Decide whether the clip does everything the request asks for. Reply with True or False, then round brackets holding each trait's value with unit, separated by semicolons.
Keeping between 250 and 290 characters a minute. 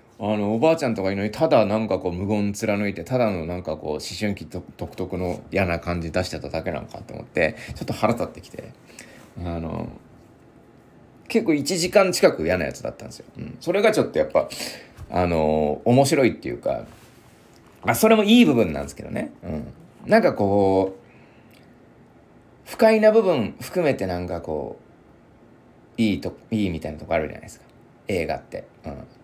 False (345 characters per minute)